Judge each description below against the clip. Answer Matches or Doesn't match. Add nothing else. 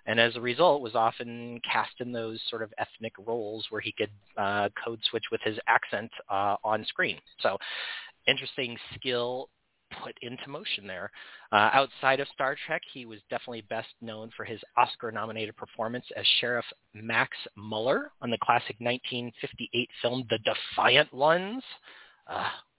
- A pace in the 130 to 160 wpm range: Matches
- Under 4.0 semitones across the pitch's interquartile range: Matches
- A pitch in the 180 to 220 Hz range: Doesn't match